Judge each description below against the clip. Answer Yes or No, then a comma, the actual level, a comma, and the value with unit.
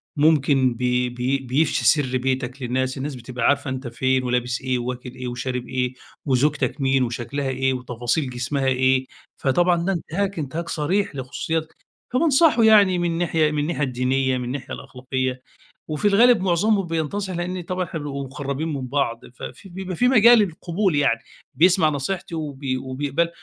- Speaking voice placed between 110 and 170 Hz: Yes, medium, 140 Hz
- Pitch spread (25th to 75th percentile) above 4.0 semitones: Yes, average, 4.8 semitones